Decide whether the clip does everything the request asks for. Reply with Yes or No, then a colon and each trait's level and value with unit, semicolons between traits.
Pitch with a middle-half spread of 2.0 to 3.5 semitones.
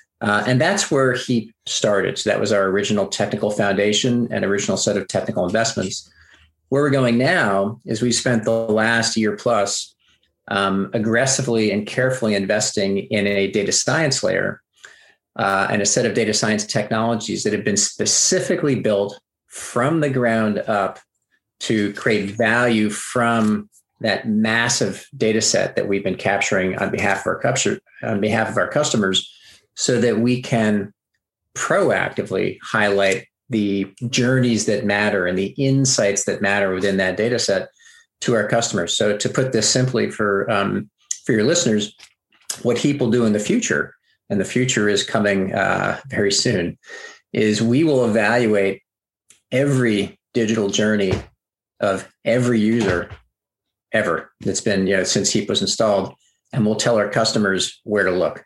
Yes: average, 3.2 semitones